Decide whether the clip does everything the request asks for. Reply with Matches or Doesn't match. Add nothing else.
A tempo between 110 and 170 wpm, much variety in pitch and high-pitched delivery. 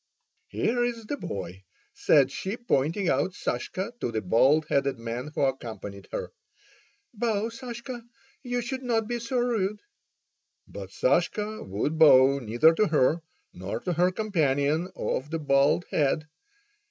Doesn't match